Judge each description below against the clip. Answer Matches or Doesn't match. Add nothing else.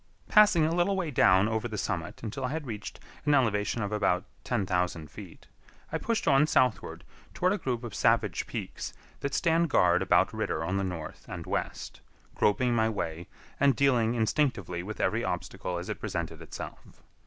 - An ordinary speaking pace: Matches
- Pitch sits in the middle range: Doesn't match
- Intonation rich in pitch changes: Matches